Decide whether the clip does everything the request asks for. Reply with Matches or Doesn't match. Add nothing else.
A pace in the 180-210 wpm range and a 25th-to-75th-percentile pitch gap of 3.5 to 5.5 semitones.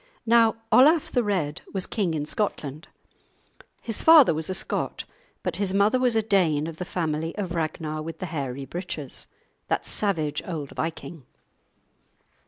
Doesn't match